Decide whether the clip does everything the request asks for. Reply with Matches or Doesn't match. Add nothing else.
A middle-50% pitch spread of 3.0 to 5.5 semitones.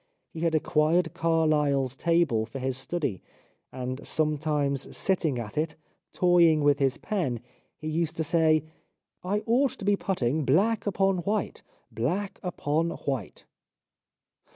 Matches